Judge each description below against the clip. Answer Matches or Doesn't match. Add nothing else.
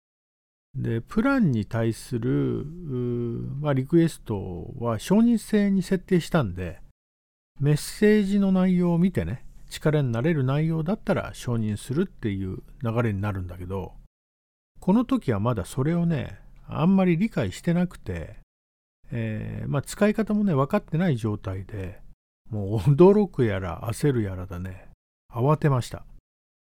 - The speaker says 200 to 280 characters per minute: Matches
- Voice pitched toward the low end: Matches